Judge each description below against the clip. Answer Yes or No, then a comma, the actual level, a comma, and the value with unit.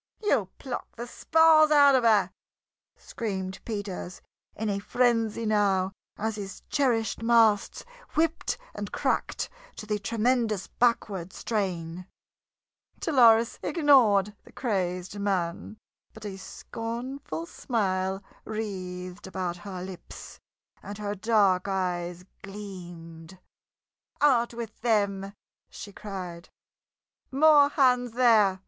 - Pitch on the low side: No, high, 210 Hz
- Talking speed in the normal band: No, slow, 105 wpm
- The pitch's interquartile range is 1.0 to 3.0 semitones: No, average, 3.8 semitones